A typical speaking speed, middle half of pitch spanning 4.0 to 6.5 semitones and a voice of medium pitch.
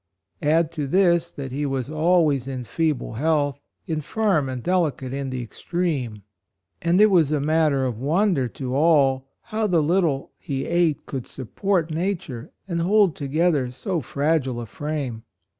Yes: average, 160 wpm; average, 4.3 semitones; medium, 150 Hz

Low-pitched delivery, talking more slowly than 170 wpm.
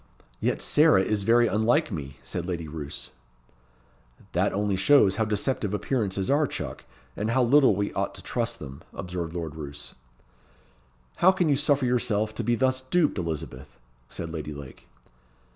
Yes: low, 105 Hz; average, 160 wpm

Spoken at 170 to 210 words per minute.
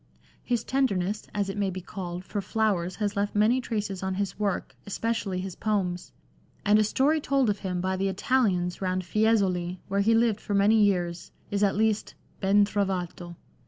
Yes: average, 180 wpm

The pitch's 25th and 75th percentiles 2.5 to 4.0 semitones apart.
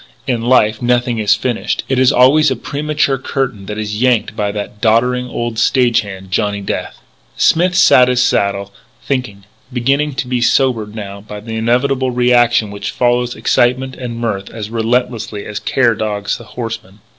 Yes: average, 3.2 semitones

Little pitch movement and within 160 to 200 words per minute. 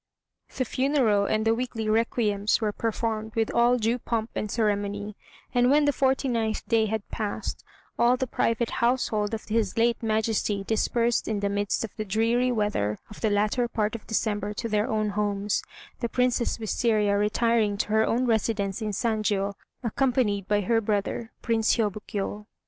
Yes: narrow, 2.1 semitones; average, 170 wpm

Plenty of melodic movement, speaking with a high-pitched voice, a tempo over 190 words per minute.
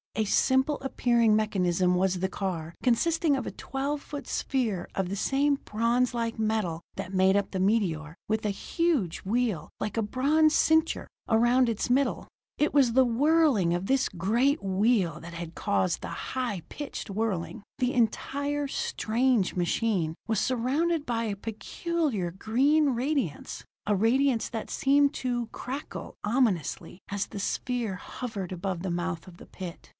No: wide, 5.8 semitones; high, 225 Hz; average, 155 wpm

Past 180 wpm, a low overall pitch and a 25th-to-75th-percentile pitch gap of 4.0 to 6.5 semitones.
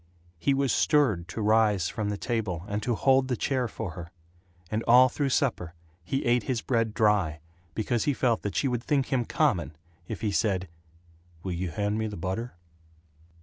Yes: average, 190 wpm; low, 110 Hz; average, 4.6 semitones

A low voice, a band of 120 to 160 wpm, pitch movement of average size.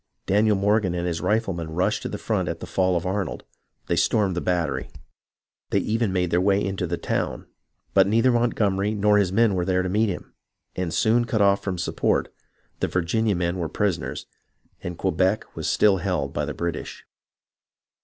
No: very low, 95 Hz; average, 185 wpm; average, 3.0 semitones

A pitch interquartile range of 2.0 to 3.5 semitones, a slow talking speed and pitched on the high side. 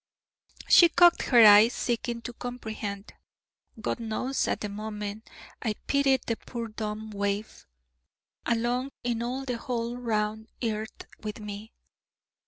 Yes: narrow, 2.4 semitones; slow, 130 wpm; high, 225 Hz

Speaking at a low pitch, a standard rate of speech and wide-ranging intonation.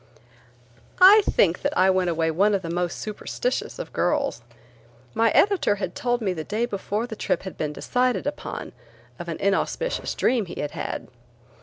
No: high, 205 Hz; average, 175 wpm; wide, 5.9 semitones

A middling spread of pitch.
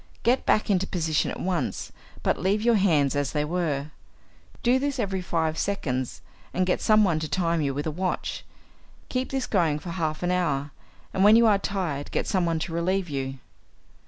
Yes: average, 4.5 semitones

